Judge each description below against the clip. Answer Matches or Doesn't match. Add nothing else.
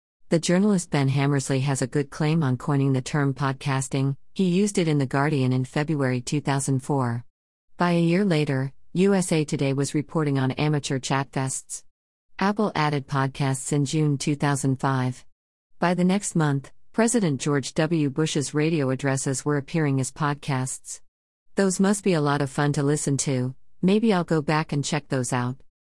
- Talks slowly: Doesn't match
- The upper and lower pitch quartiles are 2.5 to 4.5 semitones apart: Matches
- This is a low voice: Doesn't match